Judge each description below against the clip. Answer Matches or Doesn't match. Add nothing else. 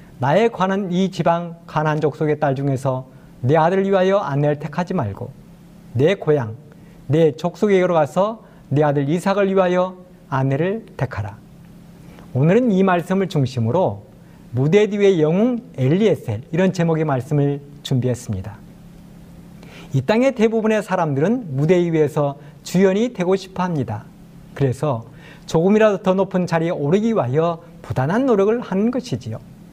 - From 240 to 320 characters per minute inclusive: Matches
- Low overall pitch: Doesn't match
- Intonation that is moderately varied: Matches